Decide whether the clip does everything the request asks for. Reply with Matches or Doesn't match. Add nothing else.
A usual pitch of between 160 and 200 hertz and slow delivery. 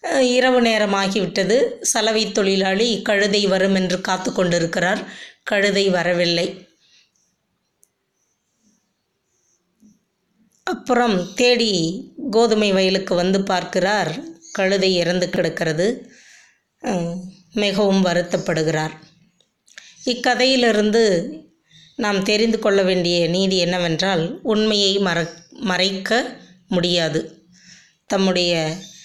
Matches